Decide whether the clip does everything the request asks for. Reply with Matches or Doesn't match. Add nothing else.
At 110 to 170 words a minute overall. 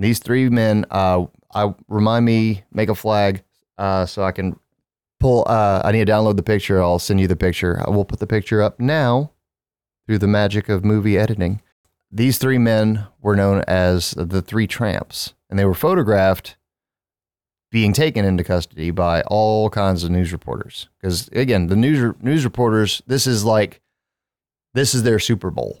Doesn't match